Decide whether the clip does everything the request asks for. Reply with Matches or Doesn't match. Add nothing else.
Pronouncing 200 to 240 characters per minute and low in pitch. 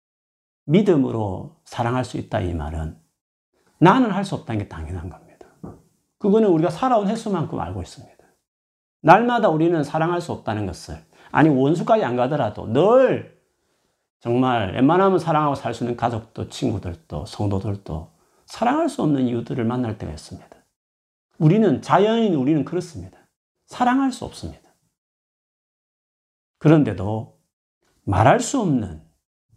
Doesn't match